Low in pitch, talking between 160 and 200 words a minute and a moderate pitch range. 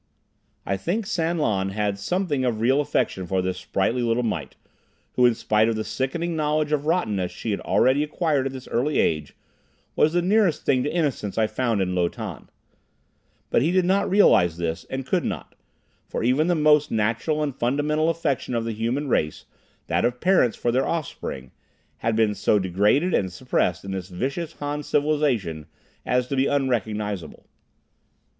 No: low, 125 Hz; average, 175 wpm; wide, 6.5 semitones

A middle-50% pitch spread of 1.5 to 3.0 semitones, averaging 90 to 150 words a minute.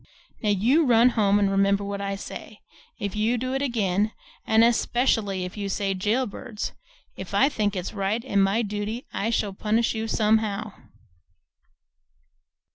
No: narrow, 2.5 semitones; average, 160 wpm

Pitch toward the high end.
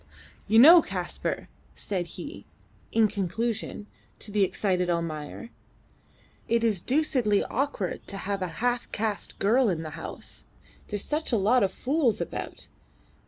Yes: high, 210 Hz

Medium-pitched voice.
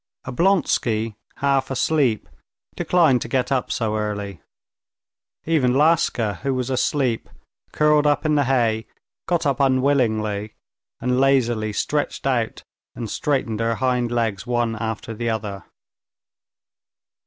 No: low, 125 Hz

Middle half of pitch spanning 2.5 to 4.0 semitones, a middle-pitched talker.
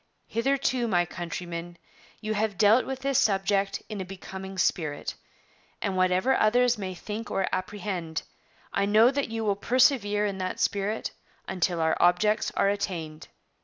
No: average, 3.1 semitones; high, 200 Hz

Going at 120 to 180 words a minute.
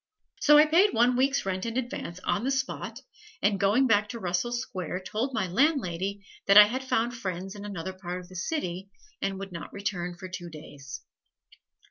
No: average, 190 wpm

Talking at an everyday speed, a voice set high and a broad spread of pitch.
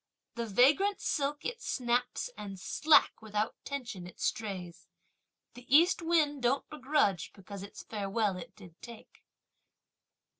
No: slow, 125 wpm; high, 235 Hz; wide, 6.5 semitones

